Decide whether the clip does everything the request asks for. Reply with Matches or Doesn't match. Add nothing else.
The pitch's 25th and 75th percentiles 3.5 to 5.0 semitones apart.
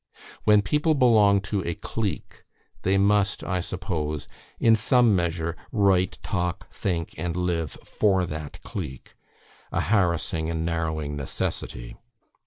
Matches